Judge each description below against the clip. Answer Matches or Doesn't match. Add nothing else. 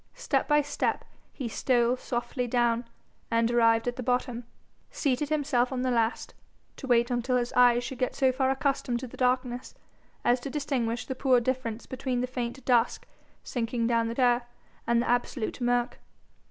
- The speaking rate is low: Doesn't match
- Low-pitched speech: Doesn't match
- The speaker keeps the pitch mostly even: Matches